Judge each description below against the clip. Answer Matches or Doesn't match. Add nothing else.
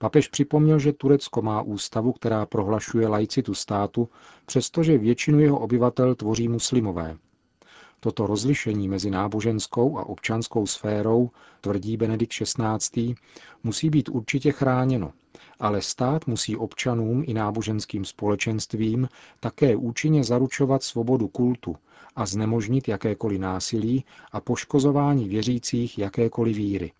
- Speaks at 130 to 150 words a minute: Doesn't match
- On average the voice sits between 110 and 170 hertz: Matches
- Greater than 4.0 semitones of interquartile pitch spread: Doesn't match